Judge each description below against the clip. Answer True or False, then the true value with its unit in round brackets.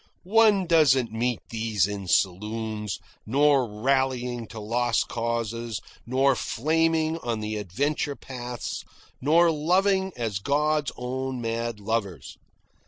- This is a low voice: True (120 Hz)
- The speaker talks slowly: True (110 wpm)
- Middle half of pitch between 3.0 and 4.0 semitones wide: False (4.9 semitones)